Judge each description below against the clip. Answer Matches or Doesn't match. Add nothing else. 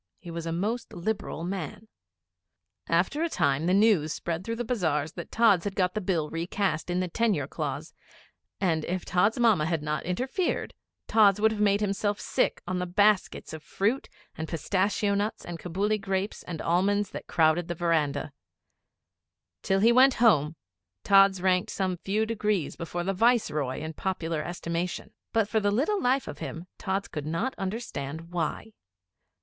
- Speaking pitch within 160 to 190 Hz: Matches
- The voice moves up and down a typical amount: Matches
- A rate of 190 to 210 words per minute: Doesn't match